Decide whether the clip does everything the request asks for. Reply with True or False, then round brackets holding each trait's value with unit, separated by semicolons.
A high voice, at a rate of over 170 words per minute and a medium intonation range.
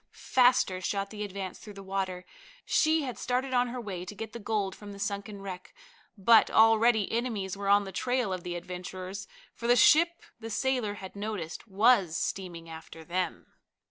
True (200 Hz; 180 wpm; 3.8 semitones)